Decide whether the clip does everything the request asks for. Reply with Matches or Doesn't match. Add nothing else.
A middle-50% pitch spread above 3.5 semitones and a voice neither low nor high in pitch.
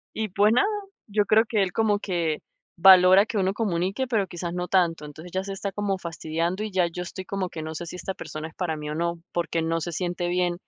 Doesn't match